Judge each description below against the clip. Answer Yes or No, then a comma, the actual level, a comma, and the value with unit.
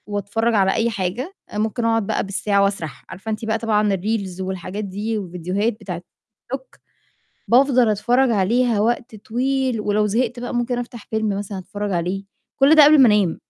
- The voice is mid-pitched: No, high, 215 Hz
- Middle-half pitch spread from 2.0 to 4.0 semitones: Yes, average, 3.3 semitones